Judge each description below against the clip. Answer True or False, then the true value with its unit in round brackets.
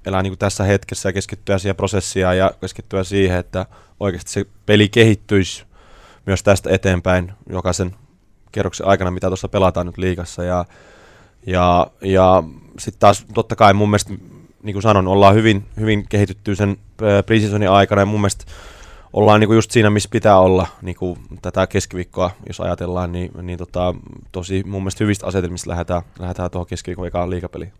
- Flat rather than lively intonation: True (2.3 semitones)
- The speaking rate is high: True (165 wpm)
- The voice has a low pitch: True (95 Hz)